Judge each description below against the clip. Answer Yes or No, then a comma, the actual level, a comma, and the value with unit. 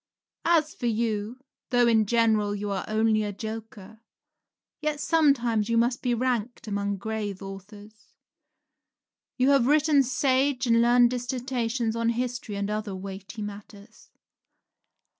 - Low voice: No, high, 230 Hz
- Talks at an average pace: No, slow, 130 wpm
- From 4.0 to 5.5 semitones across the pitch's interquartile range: No, average, 3.1 semitones